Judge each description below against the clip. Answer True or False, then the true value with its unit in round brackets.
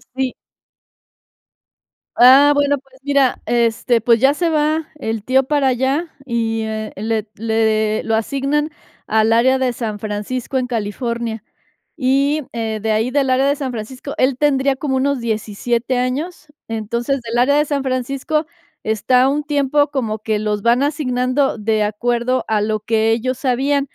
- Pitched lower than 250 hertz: False (255 Hz)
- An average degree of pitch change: True (3.7 semitones)